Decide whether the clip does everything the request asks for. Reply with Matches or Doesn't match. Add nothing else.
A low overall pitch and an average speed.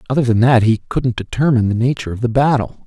Doesn't match